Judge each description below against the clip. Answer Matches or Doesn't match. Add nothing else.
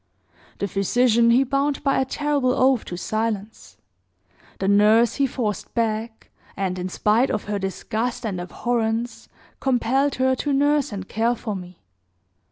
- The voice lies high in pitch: Matches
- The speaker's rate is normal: Matches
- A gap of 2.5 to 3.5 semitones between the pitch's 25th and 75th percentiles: Doesn't match